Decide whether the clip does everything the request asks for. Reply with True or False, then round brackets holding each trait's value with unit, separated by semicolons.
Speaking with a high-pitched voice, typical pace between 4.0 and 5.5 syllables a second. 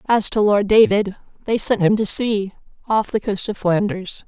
True (205 Hz; 4.5 syllables/s)